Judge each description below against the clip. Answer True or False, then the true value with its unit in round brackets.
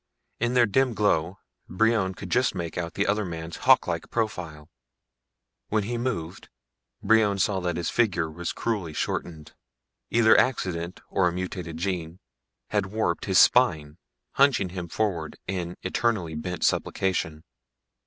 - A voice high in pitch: False (95 Hz)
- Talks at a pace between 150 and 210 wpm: False (140 wpm)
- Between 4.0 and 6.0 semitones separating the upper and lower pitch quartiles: True (4.4 semitones)